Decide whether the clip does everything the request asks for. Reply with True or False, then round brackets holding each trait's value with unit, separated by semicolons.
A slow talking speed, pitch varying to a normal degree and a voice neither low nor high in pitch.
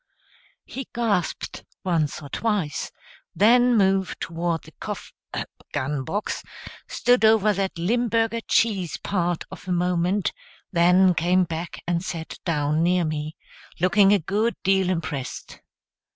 True (125 wpm; 3.7 semitones; 180 Hz)